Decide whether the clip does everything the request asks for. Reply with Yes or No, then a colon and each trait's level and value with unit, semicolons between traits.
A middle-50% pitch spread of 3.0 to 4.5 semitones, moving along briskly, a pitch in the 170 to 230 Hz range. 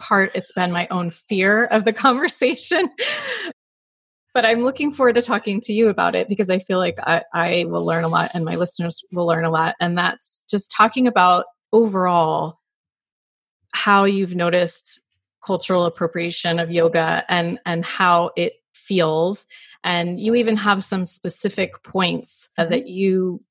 No: average, 4.2 semitones; average, 160 wpm; medium, 185 Hz